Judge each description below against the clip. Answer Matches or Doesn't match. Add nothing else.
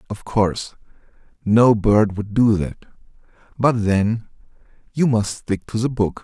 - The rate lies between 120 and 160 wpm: Matches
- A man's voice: Matches